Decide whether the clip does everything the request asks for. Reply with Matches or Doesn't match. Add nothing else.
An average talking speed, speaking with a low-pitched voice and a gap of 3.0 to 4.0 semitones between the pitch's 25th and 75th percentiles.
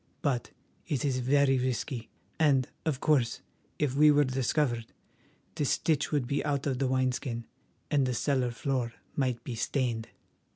Doesn't match